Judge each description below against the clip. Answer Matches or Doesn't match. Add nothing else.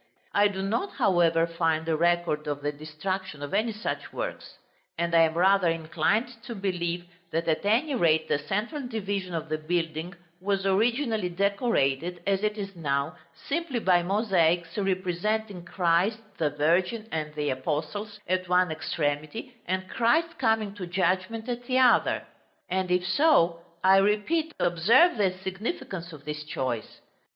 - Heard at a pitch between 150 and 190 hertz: Matches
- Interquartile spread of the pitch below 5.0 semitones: Matches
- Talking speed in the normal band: Matches